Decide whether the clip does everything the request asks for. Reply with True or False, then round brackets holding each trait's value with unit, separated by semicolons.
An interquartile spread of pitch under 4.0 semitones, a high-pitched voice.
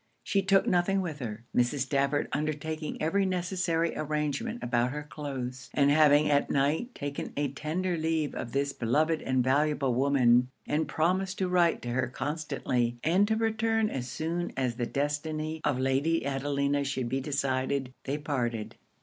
False (3.6 semitones; 145 Hz)